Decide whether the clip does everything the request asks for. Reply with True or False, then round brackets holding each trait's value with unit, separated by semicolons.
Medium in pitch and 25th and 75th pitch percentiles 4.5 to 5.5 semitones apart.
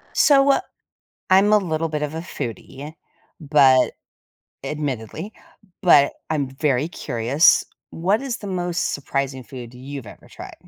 True (150 Hz; 4.9 semitones)